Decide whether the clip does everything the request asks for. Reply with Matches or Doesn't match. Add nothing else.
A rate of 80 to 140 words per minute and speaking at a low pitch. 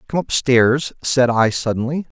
Matches